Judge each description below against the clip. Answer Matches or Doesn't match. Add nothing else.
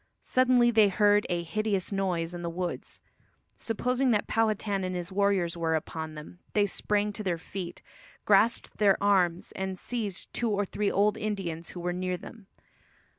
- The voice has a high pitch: Matches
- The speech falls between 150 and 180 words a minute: Matches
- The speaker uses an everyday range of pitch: Matches